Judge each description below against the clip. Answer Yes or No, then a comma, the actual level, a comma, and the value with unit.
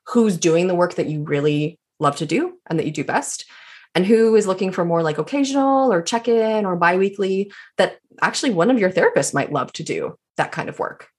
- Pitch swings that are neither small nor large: No, wide, 6.2 semitones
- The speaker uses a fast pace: Yes, fast, 230 wpm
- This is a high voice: Yes, high, 195 Hz